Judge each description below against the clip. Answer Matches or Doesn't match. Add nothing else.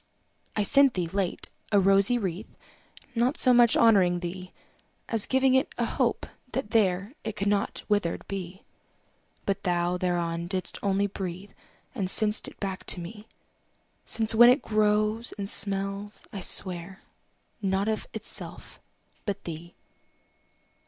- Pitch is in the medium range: Doesn't match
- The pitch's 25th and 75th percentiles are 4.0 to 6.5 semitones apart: Doesn't match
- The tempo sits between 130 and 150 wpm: Matches